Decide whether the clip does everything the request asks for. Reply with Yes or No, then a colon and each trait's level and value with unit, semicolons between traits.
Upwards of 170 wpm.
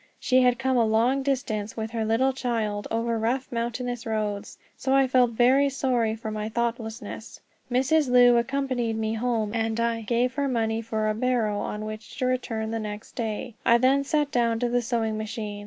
Yes: average, 190 wpm